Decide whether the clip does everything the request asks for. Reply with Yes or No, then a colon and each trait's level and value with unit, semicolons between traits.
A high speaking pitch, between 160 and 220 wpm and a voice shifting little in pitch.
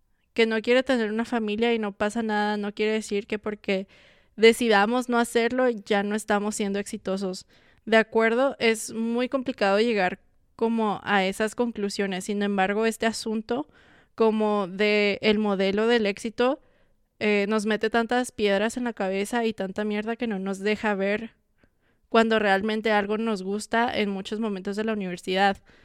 Yes: high, 215 Hz; average, 165 wpm; narrow, 2.1 semitones